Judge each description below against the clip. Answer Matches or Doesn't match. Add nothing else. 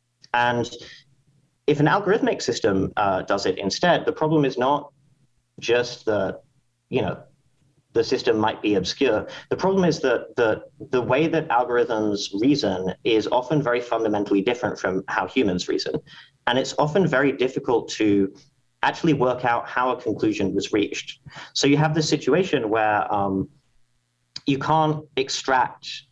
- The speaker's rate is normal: Matches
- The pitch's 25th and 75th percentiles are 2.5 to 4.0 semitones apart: Matches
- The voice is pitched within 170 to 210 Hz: Doesn't match